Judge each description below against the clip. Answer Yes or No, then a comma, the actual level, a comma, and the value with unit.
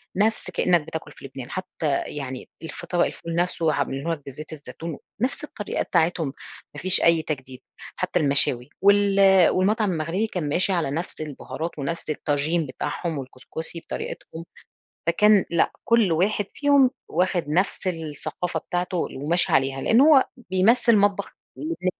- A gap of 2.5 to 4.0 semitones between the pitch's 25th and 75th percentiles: No, average, 4.4 semitones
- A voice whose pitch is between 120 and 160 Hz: No, medium, 170 Hz